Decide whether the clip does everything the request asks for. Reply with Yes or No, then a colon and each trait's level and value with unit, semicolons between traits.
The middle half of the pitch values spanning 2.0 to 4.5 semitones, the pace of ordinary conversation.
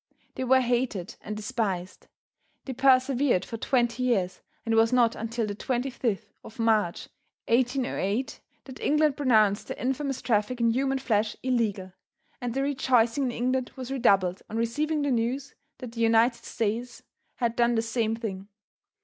Yes: average, 2.7 semitones; average, 160 wpm